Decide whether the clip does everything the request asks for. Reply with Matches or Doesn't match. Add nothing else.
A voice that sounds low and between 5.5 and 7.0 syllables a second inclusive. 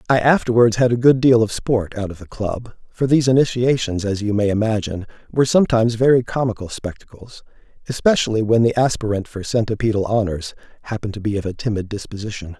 Matches